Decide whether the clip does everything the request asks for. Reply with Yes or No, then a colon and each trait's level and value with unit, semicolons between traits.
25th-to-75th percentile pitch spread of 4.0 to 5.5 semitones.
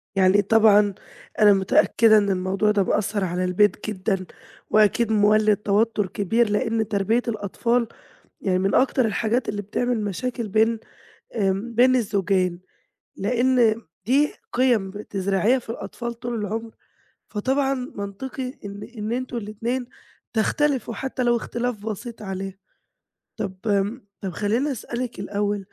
No: average, 3.1 semitones